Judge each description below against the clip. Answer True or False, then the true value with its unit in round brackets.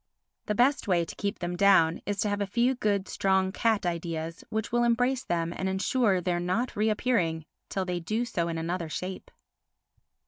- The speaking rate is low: False (185 wpm)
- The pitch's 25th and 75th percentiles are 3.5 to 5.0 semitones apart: True (4.0 semitones)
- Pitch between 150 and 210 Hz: True (190 Hz)